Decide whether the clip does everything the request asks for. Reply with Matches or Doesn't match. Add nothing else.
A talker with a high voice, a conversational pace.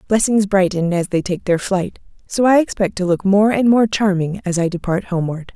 Doesn't match